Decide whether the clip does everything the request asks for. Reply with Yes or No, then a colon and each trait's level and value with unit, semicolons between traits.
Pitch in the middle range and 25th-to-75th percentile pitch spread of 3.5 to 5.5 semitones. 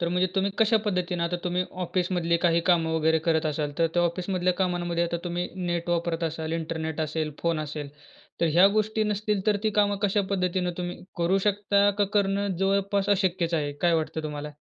No: medium, 175 Hz; average, 2.9 semitones